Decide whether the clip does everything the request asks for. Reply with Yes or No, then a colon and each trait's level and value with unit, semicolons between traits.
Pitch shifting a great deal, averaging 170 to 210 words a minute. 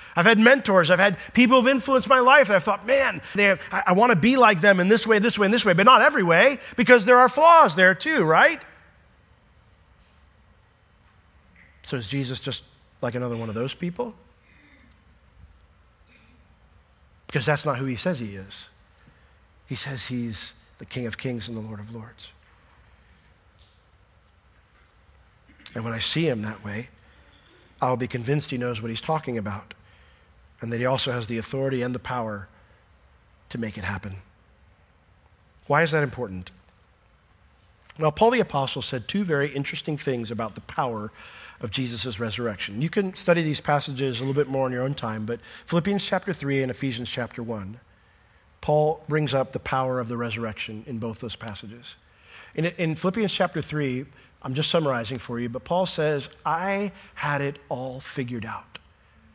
Yes: wide, 8.0 semitones; average, 175 wpm